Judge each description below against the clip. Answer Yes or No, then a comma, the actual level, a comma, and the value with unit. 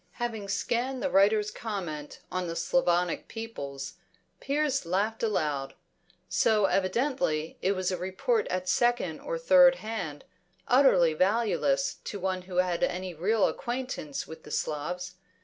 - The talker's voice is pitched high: Yes, high, 195 Hz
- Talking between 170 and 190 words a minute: No, slow, 135 wpm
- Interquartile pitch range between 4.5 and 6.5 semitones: Yes, wide, 5.4 semitones